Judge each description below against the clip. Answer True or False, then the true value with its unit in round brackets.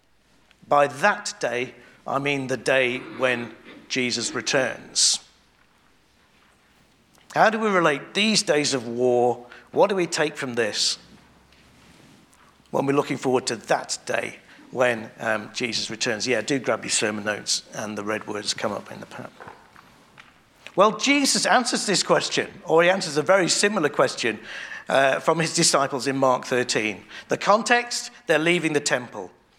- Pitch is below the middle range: False (145 Hz)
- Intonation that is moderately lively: False (7.0 semitones)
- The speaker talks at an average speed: True (155 wpm)